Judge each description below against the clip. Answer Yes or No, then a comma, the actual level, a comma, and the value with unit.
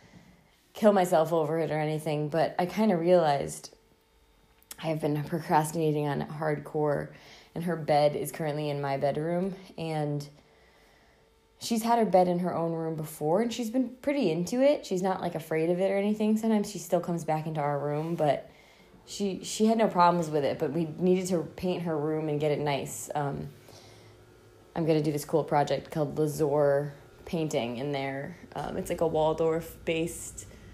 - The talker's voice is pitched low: No, medium, 160 Hz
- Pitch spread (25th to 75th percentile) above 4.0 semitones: No, average, 3.5 semitones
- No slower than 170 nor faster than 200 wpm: Yes, average, 185 wpm